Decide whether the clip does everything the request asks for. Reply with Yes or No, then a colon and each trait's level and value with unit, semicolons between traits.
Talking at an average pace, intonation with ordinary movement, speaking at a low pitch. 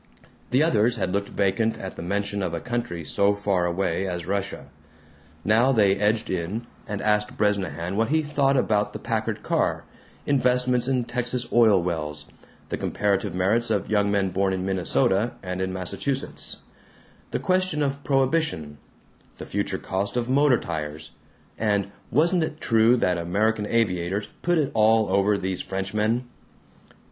Yes: average, 155 wpm; average, 4.4 semitones; low, 105 Hz